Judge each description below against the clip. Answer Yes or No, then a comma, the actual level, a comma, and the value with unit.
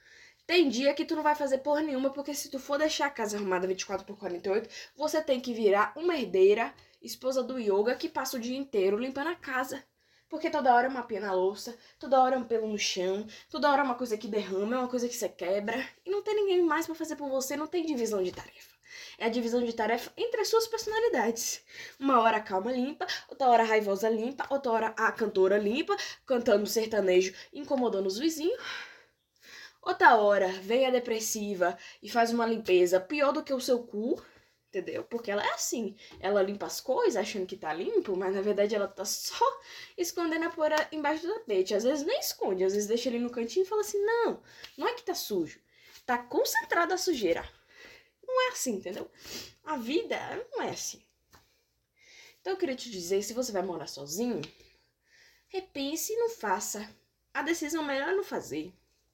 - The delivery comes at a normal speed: No, fast, 200 wpm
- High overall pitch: Yes, very high, 260 Hz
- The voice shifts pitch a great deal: Yes, wide, 8.3 semitones